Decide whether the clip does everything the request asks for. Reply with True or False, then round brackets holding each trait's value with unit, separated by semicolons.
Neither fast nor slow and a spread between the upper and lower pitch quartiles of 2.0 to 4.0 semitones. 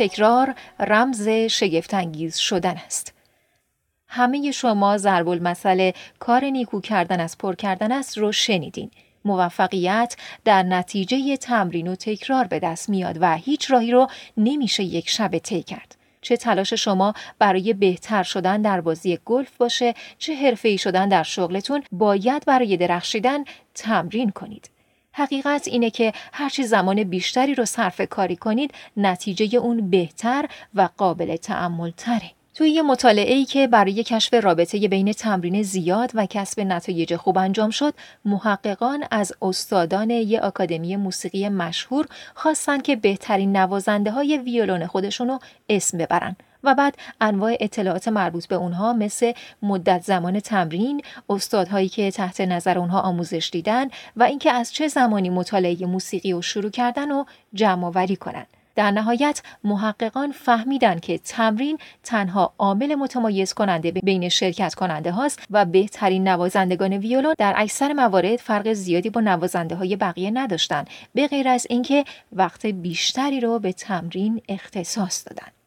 False (140 wpm; 4.5 semitones)